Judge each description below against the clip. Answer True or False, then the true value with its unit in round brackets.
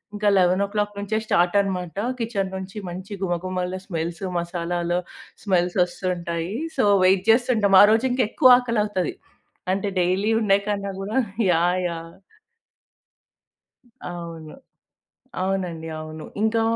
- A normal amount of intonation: True (3.0 semitones)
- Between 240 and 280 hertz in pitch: False (185 Hz)